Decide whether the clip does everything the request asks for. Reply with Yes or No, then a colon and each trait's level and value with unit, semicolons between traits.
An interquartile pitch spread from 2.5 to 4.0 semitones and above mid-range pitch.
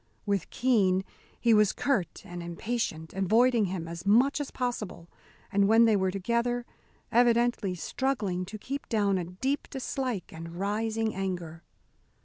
No: average, 4.7 semitones; high, 210 Hz